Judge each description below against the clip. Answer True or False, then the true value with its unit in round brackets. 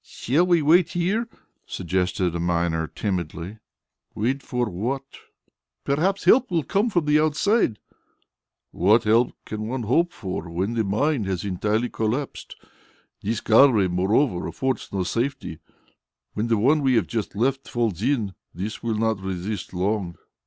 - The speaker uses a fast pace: False (145 wpm)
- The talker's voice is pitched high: False (110 Hz)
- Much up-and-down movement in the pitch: True (6.5 semitones)